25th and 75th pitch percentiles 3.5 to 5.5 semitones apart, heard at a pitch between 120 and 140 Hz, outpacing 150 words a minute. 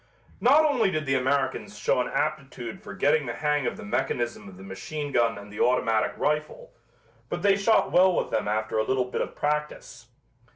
Yes: average, 4.7 semitones; low, 135 Hz; average, 200 wpm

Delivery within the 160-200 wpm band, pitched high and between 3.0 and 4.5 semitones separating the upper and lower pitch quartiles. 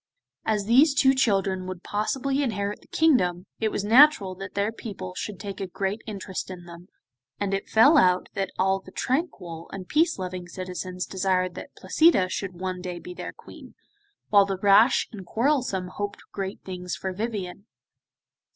Yes: average, 170 wpm; high, 195 Hz; average, 3.3 semitones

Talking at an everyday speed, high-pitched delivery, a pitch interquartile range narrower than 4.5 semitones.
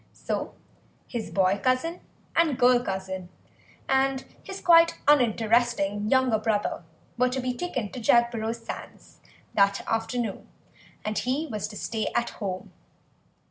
No: slow, 130 wpm; high, 235 Hz; average, 3.7 semitones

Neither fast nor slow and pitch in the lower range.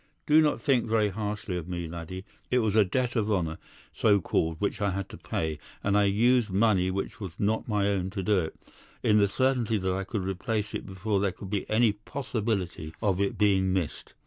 No: fast, 215 wpm; low, 100 Hz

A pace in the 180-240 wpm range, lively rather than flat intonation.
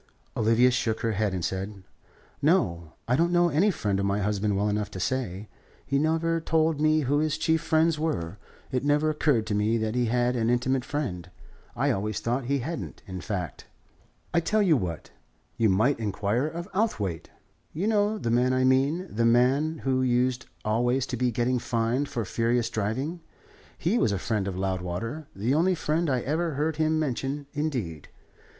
Yes: average, 185 wpm; wide, 6.4 semitones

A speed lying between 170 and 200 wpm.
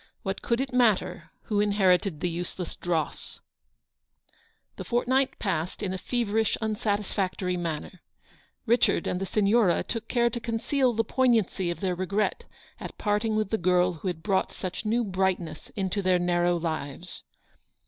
No: average, 160 wpm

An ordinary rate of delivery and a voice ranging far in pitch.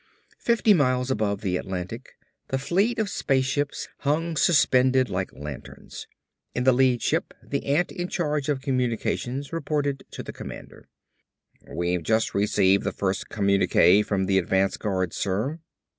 Yes: average, 145 wpm; wide, 6.6 semitones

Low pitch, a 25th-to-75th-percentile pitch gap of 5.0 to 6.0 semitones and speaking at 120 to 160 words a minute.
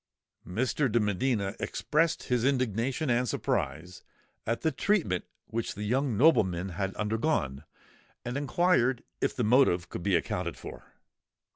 Yes: low, 115 Hz; wide, 5.6 semitones; slow, 135 wpm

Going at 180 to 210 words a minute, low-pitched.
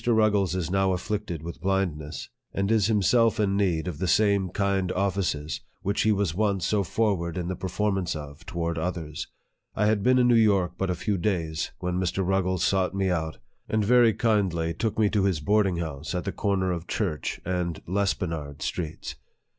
Yes: average, 185 wpm; very low, 95 Hz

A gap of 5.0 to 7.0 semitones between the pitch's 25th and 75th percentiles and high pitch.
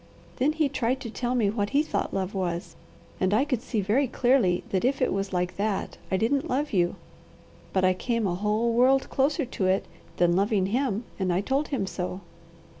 Yes: wide, 5.6 semitones; high, 215 Hz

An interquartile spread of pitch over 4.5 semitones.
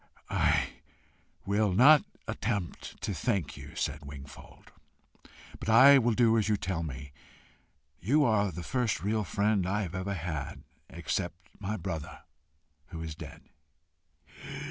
Yes: average, 5.1 semitones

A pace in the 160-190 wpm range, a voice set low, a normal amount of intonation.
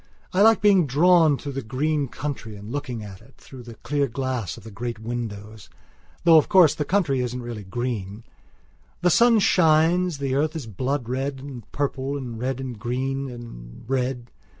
Yes: average, 180 wpm; low, 130 Hz; average, 3.9 semitones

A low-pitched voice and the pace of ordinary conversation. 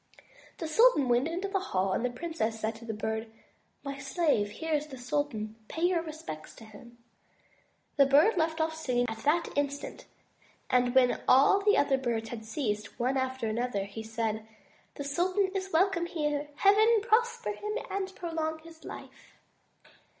No: very high, 285 Hz; average, 170 wpm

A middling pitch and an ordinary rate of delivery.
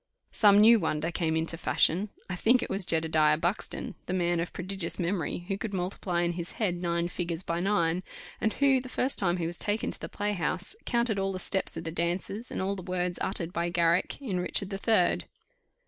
No: medium, 180 Hz; fast, 210 wpm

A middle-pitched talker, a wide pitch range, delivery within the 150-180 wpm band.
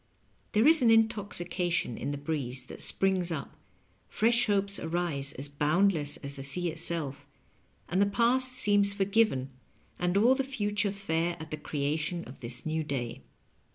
Yes: medium, 175 Hz; wide, 6.0 semitones; average, 155 wpm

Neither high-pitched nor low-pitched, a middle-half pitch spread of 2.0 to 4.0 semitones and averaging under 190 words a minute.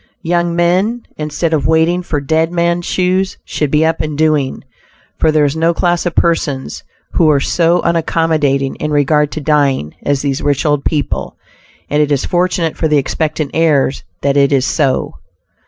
Yes: medium, 155 Hz; average, 2.8 semitones; average, 175 wpm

